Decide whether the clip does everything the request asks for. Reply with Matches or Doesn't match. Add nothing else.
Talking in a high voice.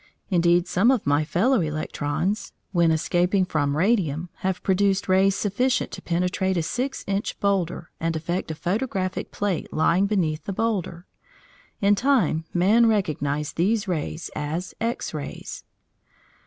Doesn't match